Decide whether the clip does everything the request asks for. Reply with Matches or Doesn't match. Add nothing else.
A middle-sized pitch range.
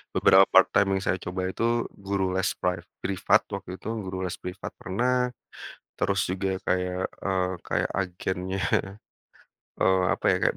Doesn't match